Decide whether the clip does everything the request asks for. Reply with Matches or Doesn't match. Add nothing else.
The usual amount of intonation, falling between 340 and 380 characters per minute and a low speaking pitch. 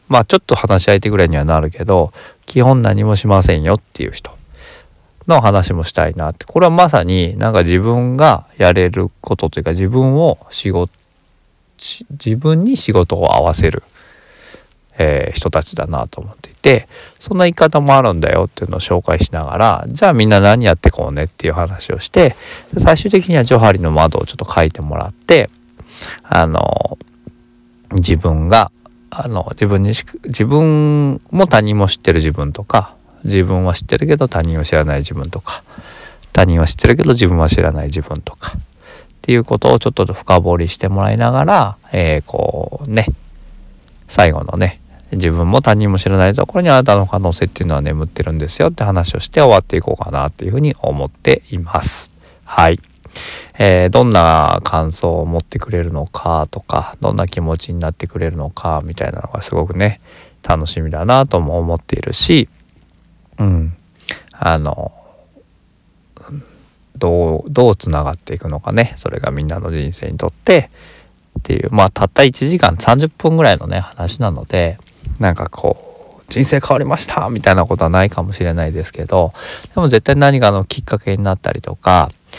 Doesn't match